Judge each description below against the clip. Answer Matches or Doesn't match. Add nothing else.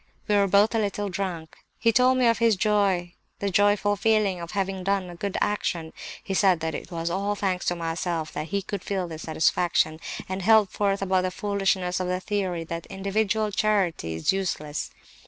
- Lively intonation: Doesn't match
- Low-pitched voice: Doesn't match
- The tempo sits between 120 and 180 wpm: Doesn't match